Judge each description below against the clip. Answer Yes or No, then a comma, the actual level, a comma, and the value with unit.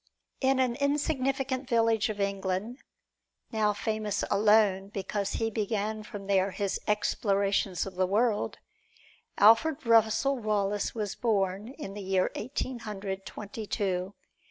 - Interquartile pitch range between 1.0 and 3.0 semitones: Yes, narrow, 2.6 semitones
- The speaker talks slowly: Yes, slow, 130 wpm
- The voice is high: Yes, high, 210 Hz